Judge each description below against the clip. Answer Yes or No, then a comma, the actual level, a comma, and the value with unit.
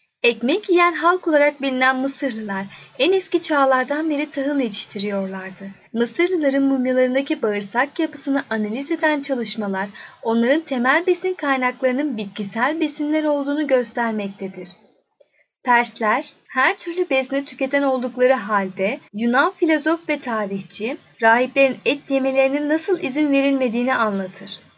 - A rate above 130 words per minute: No, average, 110 wpm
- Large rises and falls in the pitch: No, average, 4.7 semitones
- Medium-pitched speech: No, very high, 265 Hz